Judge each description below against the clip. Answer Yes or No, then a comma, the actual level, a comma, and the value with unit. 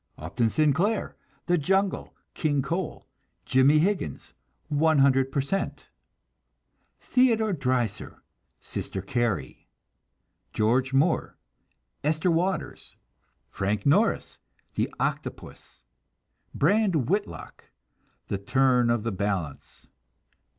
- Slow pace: Yes, slow, 85 wpm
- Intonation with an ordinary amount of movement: No, wide, 7.1 semitones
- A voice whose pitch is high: No, medium, 140 Hz